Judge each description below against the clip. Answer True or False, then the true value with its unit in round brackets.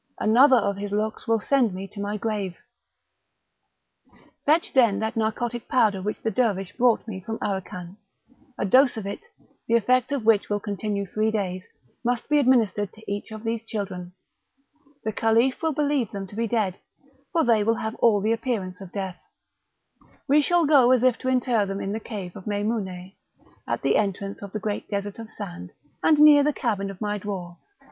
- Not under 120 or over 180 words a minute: False (190 wpm)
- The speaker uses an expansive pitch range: False (3.3 semitones)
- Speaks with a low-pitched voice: False (215 Hz)